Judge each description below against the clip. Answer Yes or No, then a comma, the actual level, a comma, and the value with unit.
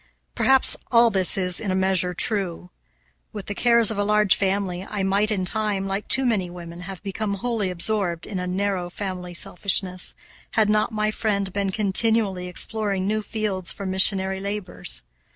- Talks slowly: No, average, 170 wpm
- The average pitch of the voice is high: Yes, high, 195 Hz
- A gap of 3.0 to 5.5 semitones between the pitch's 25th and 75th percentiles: No, narrow, 2.5 semitones